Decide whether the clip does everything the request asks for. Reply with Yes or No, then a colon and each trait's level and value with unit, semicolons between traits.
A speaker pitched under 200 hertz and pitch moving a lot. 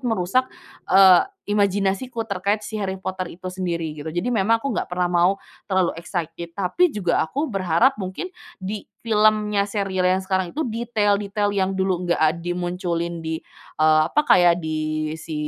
No: high, 190 Hz; average, 3.3 semitones